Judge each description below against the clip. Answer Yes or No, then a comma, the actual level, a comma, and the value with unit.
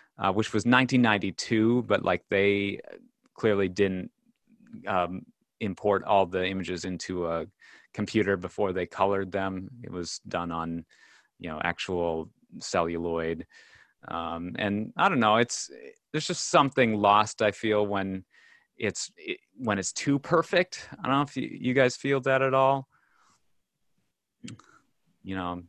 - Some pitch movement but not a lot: No, wide, 6.0 semitones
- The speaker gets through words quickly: No, average, 145 wpm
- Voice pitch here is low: Yes, low, 100 Hz